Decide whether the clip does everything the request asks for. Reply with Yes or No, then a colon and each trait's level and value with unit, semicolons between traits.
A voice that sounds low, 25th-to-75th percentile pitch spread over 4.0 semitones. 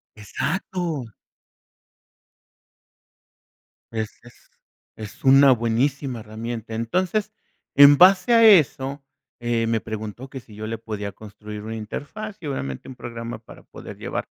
Yes: low, 120 Hz; average, 4.7 semitones